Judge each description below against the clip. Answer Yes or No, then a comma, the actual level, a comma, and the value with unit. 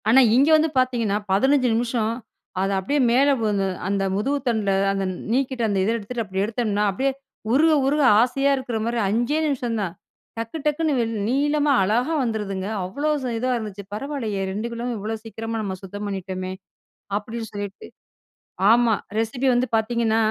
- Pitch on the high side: Yes, high, 230 Hz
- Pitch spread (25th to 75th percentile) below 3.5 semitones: No, average, 4.1 semitones